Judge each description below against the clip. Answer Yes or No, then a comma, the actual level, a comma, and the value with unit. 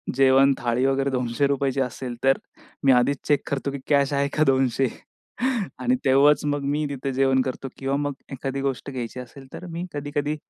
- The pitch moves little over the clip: Yes, narrow, 1.3 semitones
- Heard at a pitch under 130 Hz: No, low, 135 Hz